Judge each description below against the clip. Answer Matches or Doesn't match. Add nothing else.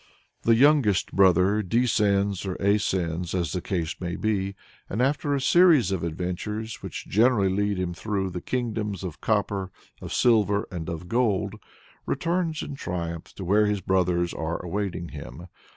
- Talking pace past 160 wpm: Doesn't match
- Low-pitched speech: Matches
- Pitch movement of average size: Matches